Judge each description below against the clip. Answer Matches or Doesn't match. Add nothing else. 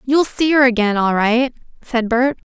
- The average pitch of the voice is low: Doesn't match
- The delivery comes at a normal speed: Matches